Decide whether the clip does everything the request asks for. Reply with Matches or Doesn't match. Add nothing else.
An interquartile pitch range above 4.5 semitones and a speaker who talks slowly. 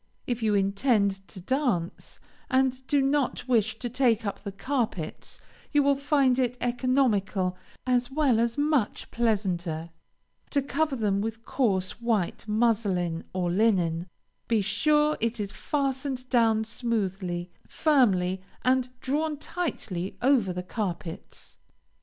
Matches